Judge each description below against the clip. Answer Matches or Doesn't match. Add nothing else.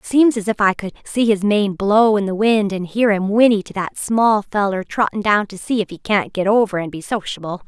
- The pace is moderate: Doesn't match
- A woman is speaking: Matches